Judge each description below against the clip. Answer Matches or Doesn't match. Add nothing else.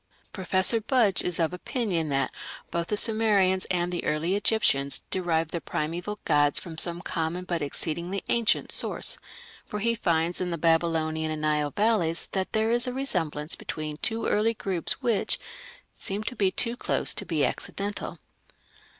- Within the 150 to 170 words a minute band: Matches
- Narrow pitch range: Doesn't match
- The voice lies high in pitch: Doesn't match